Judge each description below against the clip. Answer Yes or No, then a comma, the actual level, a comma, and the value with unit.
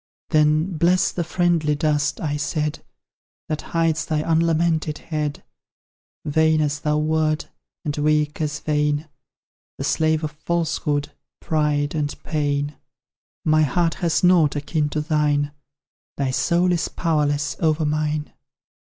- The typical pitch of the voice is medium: Yes, medium, 155 Hz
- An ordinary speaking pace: No, slow, 125 wpm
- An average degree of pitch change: No, narrow, 1.4 semitones